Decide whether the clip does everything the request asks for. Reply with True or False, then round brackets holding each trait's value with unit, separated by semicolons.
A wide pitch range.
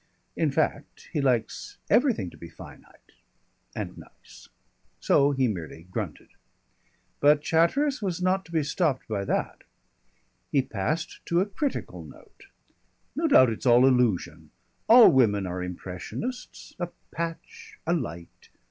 True (8.9 semitones)